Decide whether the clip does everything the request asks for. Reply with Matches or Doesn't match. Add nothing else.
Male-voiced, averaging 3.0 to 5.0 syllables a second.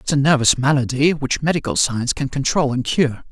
Doesn't match